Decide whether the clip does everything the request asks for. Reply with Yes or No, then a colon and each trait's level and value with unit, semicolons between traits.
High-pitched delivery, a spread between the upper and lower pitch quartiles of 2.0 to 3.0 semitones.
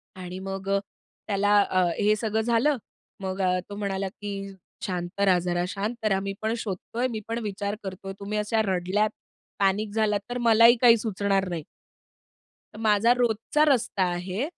Yes: high, 205 Hz; narrow, 2.5 semitones